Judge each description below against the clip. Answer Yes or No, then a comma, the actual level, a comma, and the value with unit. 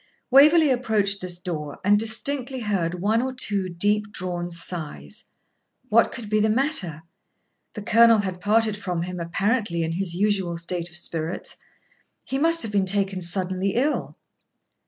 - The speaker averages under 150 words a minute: No, average, 155 wpm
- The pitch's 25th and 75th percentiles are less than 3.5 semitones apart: No, average, 4.4 semitones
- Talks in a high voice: Yes, high, 200 Hz